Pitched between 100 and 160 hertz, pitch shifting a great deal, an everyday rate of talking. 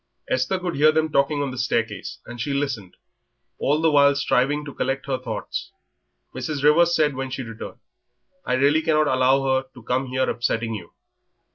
No: low, 135 Hz; average, 2.8 semitones; average, 180 wpm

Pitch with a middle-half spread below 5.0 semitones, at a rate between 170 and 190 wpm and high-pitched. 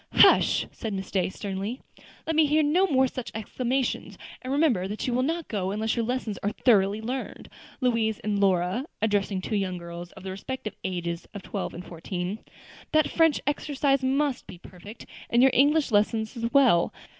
No: wide, 5.5 semitones; average, 180 wpm; high, 220 Hz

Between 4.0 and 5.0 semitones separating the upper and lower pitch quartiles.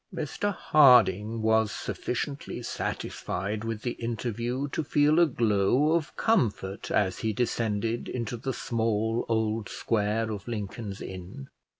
No: average, 3.1 semitones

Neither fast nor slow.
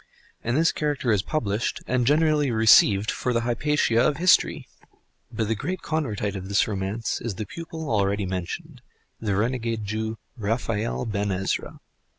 Yes: average, 155 wpm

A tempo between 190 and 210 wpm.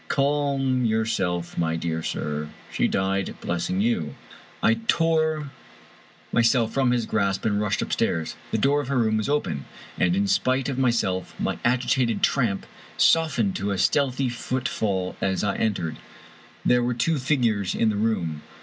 No: average, 160 wpm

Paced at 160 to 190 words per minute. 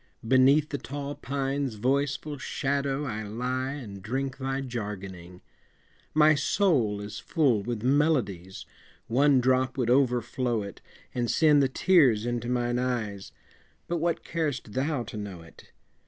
No: average, 140 wpm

